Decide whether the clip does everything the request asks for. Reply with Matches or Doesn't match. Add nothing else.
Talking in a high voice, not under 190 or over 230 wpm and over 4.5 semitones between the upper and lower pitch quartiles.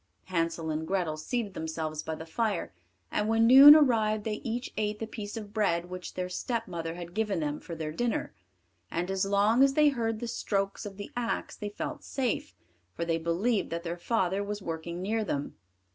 Matches